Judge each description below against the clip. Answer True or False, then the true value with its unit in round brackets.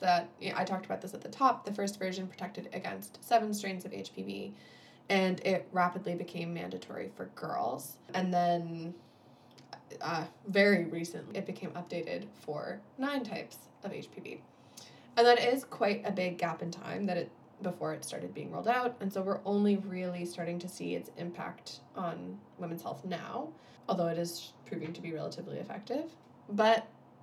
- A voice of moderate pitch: True (180 Hz)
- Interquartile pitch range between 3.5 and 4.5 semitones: False (2.9 semitones)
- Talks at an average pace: True (175 wpm)